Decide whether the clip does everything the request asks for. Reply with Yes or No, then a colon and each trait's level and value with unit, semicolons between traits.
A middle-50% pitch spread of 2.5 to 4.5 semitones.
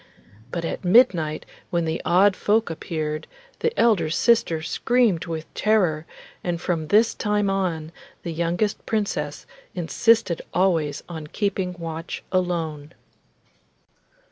Yes: average, 4.2 semitones